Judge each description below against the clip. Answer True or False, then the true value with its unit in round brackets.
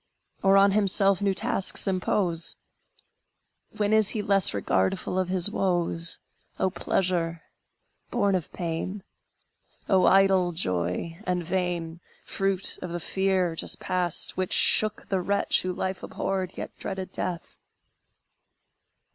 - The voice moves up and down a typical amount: False (2.1 semitones)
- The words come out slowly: True (125 wpm)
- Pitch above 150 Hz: True (185 Hz)